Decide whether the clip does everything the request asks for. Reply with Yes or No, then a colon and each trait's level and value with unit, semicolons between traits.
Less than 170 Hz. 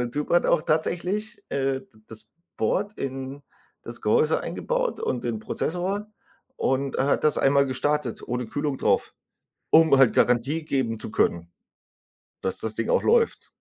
Yes: medium, 140 Hz